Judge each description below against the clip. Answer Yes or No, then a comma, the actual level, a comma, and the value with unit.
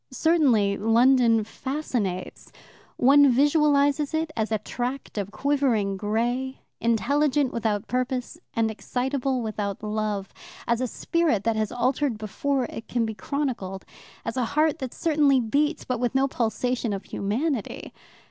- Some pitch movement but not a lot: Yes, average, 4.4 semitones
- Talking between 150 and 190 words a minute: No, average, 140 wpm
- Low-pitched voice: No, high, 245 Hz